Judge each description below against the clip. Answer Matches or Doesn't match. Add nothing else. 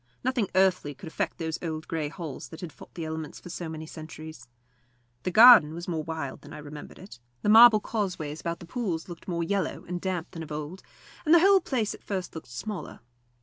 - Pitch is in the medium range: Matches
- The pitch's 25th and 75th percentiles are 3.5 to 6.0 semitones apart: Matches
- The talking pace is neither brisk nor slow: Doesn't match